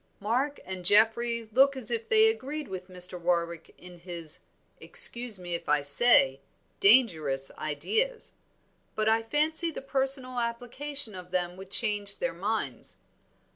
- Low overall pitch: No, high, 220 Hz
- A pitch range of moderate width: No, wide, 7.2 semitones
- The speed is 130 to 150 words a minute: Yes, average, 140 wpm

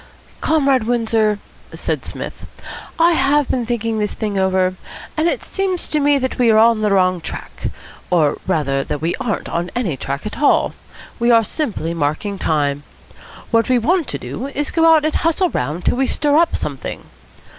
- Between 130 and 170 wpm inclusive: No, average, 185 wpm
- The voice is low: No, high, 230 Hz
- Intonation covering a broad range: Yes, wide, 7.9 semitones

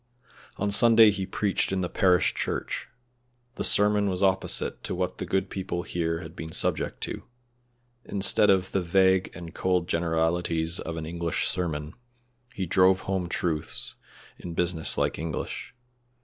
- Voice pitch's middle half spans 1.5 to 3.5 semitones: Yes, narrow, 2.5 semitones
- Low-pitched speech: Yes, very low, 90 Hz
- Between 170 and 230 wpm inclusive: No, average, 155 wpm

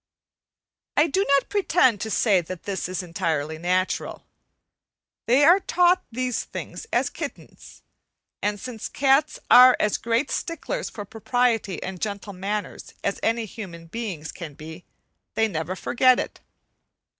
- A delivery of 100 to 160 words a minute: Yes, average, 140 wpm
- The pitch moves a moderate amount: No, wide, 5.7 semitones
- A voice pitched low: No, high, 215 Hz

